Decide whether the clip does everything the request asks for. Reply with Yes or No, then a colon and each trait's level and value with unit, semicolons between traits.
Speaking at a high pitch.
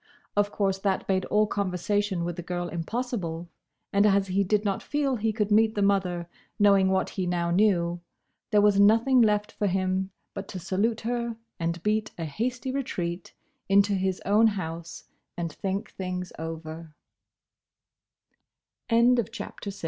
Yes: high, 195 Hz